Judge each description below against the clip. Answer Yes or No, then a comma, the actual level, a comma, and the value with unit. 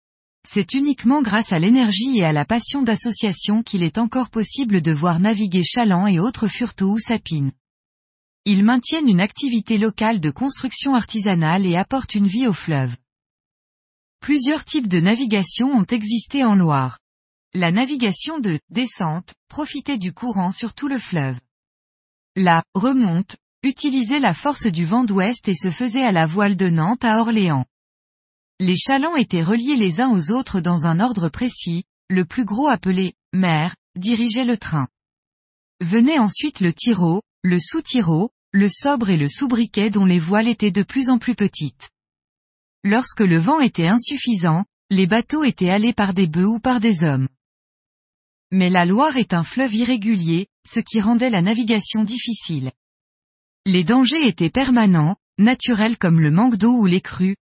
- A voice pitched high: Yes, high, 210 Hz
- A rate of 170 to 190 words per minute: No, average, 160 wpm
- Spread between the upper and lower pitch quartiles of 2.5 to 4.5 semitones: No, wide, 5.6 semitones